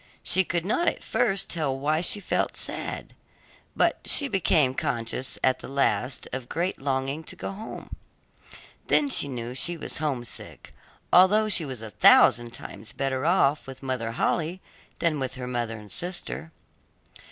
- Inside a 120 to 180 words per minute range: Yes, average, 155 wpm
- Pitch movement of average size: No, wide, 5.7 semitones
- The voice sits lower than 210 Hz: Yes, medium, 140 Hz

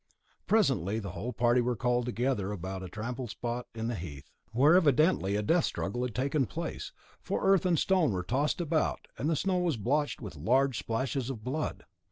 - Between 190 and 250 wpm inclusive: Yes, average, 195 wpm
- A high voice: No, low, 125 Hz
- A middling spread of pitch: No, wide, 5.7 semitones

